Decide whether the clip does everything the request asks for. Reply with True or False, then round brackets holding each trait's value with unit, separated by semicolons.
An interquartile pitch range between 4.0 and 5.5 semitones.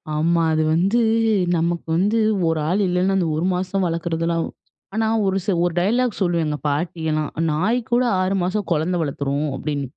False (3.3 semitones)